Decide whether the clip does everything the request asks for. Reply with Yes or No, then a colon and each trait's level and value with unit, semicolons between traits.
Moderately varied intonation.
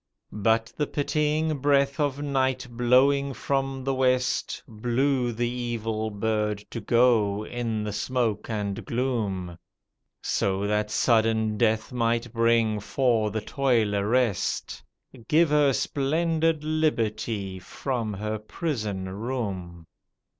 Yes: average, 4.0 semitones